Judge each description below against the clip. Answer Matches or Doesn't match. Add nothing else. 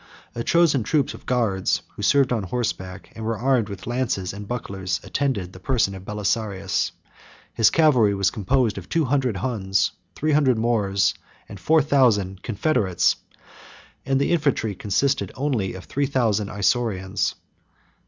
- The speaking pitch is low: Matches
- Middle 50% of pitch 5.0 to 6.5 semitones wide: Matches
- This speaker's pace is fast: Doesn't match